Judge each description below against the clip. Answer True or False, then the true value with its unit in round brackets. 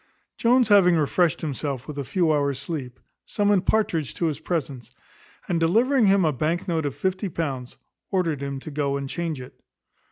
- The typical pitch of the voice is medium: True (160 Hz)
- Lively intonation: False (4.9 semitones)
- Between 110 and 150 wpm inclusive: False (180 wpm)